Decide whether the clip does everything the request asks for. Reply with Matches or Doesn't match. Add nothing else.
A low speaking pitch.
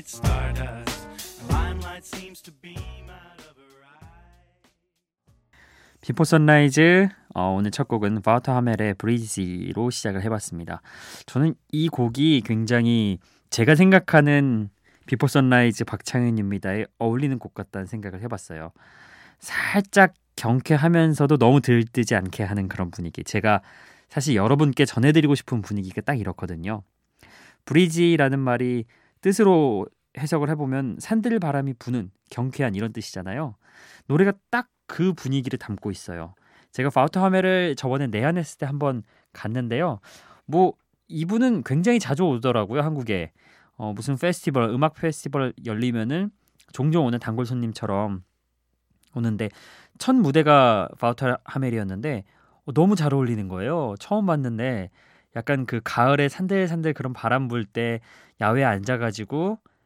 Matches